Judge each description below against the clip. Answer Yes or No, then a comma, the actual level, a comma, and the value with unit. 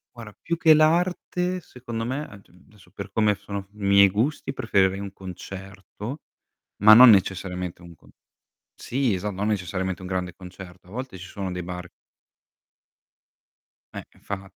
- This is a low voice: Yes, low, 100 Hz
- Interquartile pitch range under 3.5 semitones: No, average, 4.0 semitones